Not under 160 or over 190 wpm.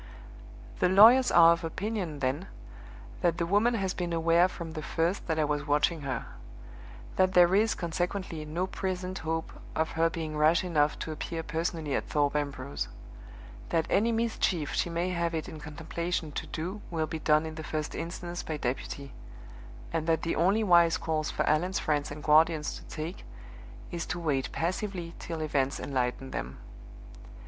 Yes: average, 175 wpm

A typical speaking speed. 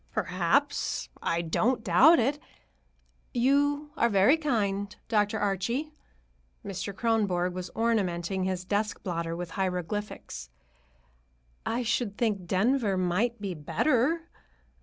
No: slow, 110 wpm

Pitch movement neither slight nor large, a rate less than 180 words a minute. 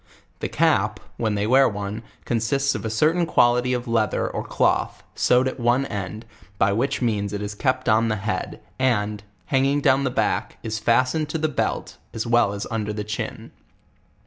No: average, 3.7 semitones; average, 190 wpm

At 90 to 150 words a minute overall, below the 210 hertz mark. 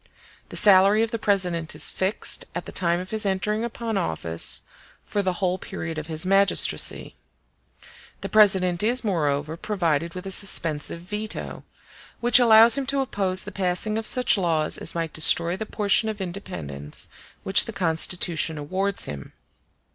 No: average, 160 wpm; high, 190 Hz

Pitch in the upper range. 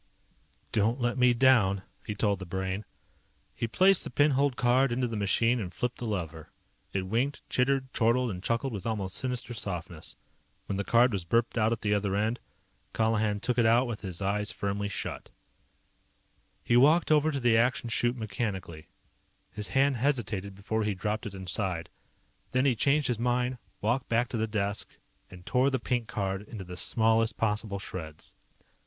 No: low, 110 Hz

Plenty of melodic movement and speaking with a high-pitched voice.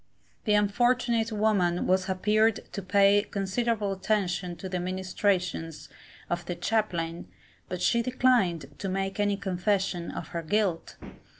No: average, 3.0 semitones; high, 195 Hz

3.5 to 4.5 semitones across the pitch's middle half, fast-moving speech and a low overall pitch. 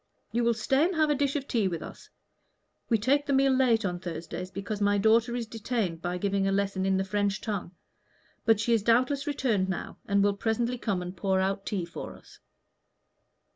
No: average, 4.0 semitones; fast, 210 wpm; high, 210 Hz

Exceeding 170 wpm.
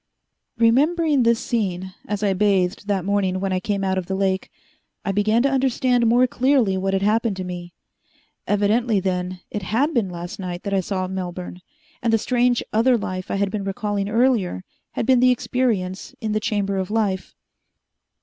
Yes: average, 185 wpm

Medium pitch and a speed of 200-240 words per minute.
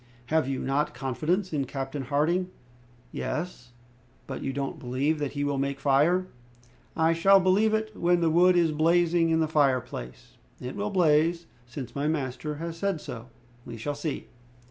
No: medium, 150 Hz; average, 165 wpm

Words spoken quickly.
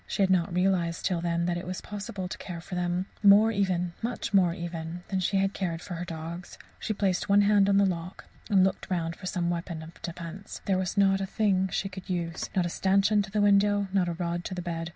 Yes: fast, 245 wpm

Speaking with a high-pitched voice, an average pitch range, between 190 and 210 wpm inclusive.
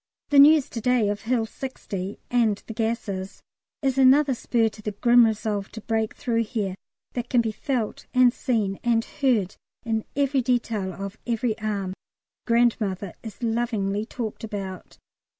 No: high, 225 Hz; average, 3.0 semitones; average, 155 wpm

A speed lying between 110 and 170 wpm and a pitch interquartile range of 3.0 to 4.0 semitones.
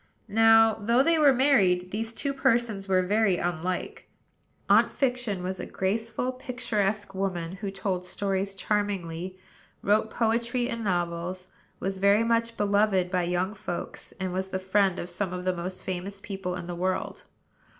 Yes: average, 160 wpm; average, 3.5 semitones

